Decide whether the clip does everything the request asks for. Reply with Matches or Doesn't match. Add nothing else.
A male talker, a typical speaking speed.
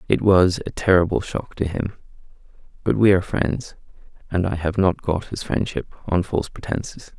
Matches